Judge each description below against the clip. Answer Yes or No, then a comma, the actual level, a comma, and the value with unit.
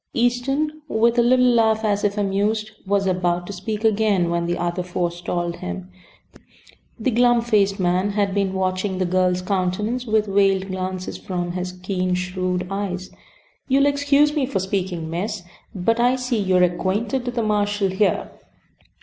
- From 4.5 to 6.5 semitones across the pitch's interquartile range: No, average, 3.6 semitones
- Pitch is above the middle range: Yes, high, 195 Hz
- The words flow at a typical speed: Yes, average, 160 wpm